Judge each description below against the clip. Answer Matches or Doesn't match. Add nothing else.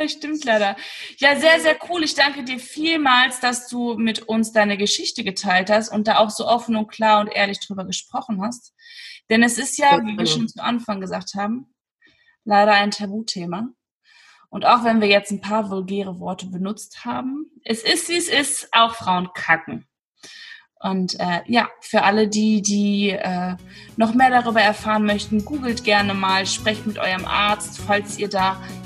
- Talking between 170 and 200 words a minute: Matches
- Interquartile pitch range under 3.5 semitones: Doesn't match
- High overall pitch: Matches